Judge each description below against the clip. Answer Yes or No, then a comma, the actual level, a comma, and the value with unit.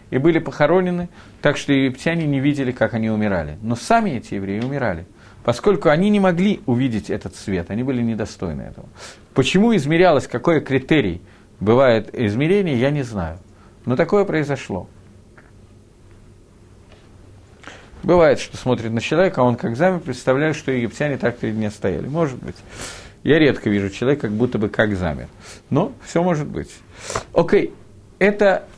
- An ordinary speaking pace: Yes, average, 150 wpm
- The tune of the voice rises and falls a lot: Yes, wide, 6.3 semitones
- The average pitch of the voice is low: Yes, low, 120 Hz